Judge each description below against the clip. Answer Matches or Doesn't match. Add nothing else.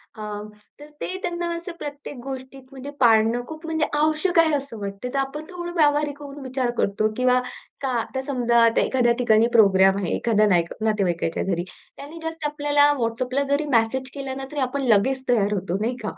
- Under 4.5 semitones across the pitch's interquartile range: Doesn't match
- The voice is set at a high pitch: Matches